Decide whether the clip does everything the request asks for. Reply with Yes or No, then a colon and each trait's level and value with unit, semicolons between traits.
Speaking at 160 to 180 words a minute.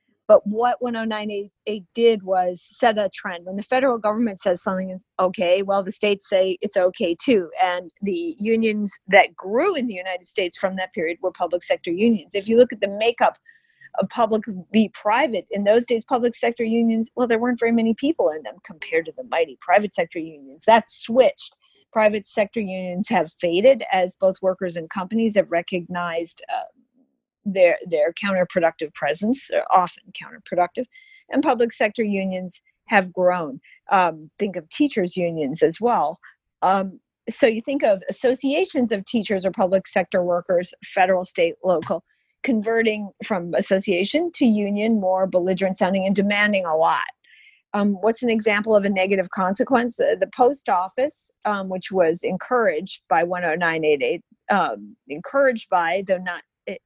Yes: average, 165 wpm